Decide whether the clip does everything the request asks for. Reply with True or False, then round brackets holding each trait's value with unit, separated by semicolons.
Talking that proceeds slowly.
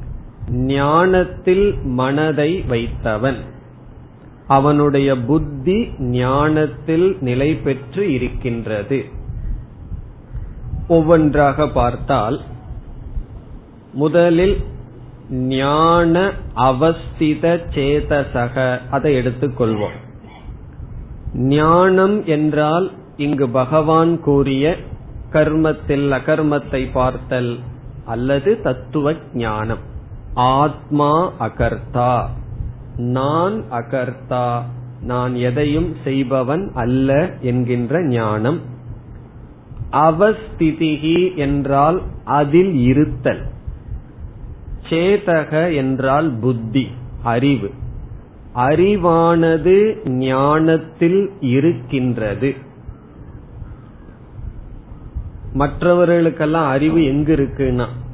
True (55 wpm)